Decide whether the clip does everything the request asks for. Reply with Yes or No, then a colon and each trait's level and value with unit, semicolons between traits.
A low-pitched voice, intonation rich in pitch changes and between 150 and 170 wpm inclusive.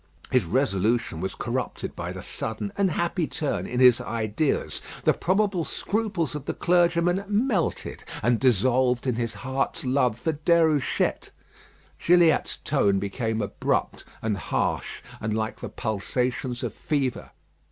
No: low, 130 Hz; wide, 6.8 semitones; slow, 135 wpm